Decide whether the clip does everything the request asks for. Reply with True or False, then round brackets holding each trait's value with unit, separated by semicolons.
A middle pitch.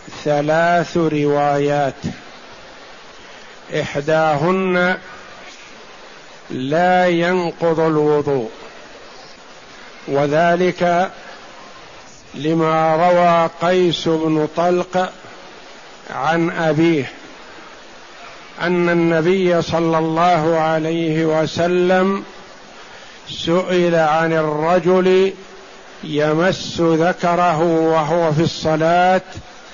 True (165 Hz)